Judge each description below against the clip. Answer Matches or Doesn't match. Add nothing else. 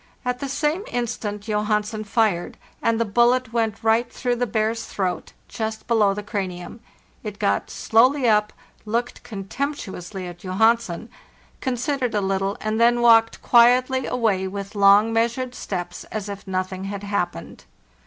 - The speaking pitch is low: Doesn't match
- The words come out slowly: Doesn't match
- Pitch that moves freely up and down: Doesn't match